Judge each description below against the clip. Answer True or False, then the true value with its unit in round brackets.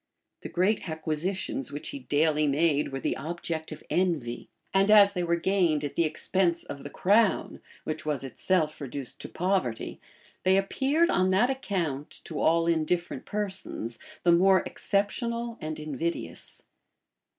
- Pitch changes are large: False (4.2 semitones)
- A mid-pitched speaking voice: True (170 Hz)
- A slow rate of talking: False (150 wpm)